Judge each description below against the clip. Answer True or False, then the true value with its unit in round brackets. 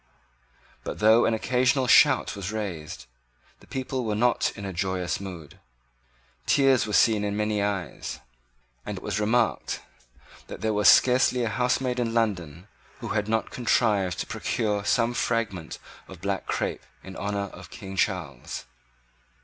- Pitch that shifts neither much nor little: True (3.6 semitones)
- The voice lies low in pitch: True (105 Hz)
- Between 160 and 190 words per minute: False (150 wpm)